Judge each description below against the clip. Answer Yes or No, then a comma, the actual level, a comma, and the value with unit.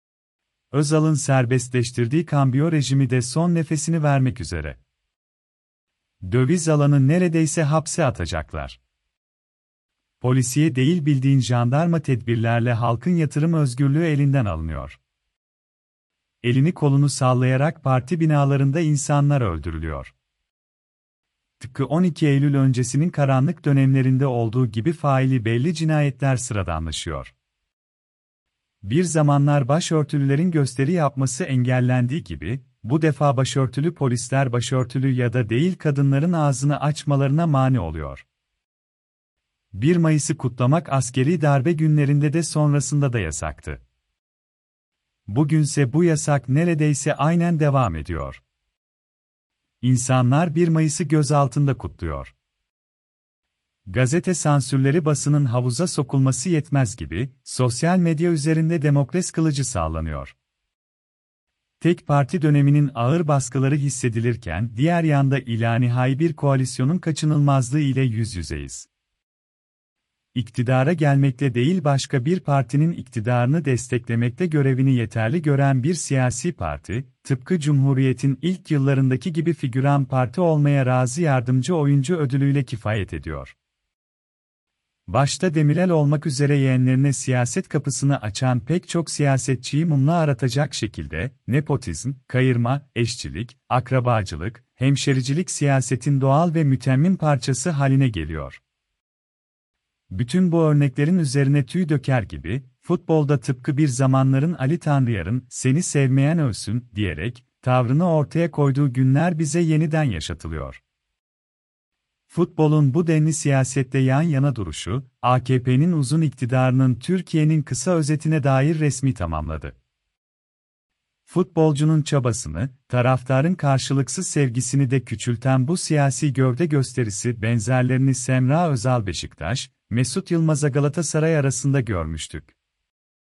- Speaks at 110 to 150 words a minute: No, average, 100 wpm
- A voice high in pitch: No, low, 135 Hz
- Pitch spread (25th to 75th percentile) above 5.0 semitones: No, average, 3.9 semitones